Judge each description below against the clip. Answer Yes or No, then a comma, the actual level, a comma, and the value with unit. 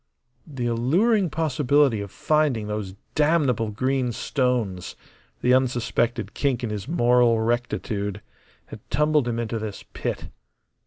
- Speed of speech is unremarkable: No, slow, 120 wpm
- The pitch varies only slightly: No, average, 4.2 semitones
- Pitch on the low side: Yes, low, 120 Hz